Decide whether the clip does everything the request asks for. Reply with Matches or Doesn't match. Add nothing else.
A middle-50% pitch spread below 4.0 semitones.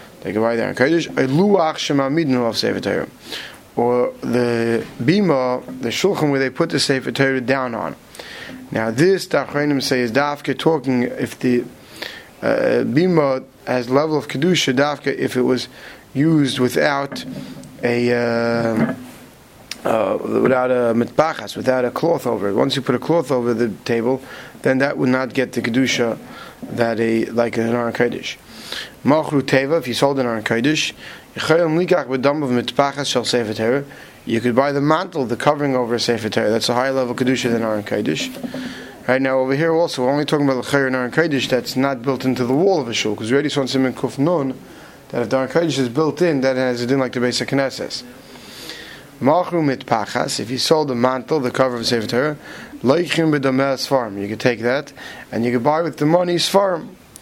Matches